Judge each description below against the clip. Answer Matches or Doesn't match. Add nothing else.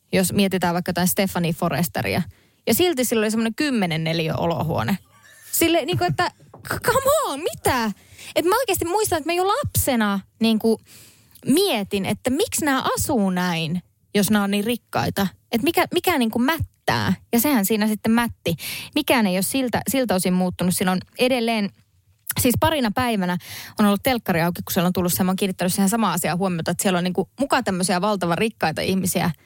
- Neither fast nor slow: Doesn't match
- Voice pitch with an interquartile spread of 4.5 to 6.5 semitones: Matches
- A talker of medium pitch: Doesn't match